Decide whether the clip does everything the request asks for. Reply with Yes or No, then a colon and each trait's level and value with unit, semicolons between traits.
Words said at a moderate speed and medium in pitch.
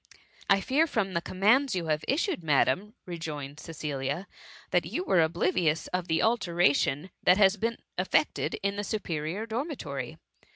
Yes: average, 170 wpm; medium, 180 Hz